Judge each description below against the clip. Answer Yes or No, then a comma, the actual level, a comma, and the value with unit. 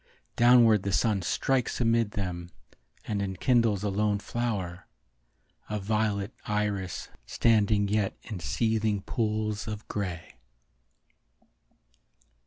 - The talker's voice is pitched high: No, low, 105 Hz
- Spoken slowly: Yes, slow, 100 wpm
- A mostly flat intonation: Yes, narrow, 2.1 semitones